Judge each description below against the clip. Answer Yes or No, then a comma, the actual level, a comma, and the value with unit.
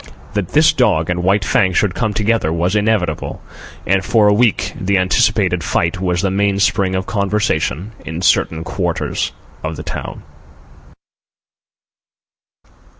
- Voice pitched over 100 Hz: No, very low, 95 Hz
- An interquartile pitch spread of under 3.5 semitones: Yes, average, 2.8 semitones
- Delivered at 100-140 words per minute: Yes, slow, 135 wpm